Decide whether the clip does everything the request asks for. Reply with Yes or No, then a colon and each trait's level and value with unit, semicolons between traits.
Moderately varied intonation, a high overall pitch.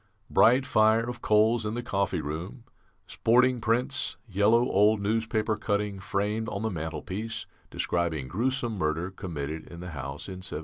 No: average, 4.4 semitones; low, 105 Hz